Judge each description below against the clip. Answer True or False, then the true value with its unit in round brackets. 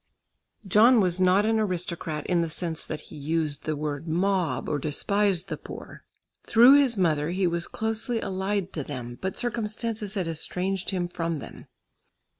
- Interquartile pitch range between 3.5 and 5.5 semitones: True (4.4 semitones)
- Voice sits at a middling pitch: True (180 Hz)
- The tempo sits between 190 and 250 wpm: False (165 wpm)